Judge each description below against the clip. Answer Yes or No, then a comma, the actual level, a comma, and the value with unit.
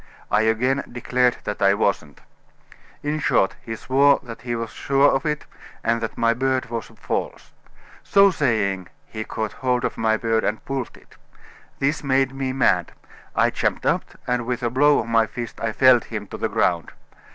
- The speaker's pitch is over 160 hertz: No, low, 120 Hz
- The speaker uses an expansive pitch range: No, average, 3.2 semitones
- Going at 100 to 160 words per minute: No, average, 185 wpm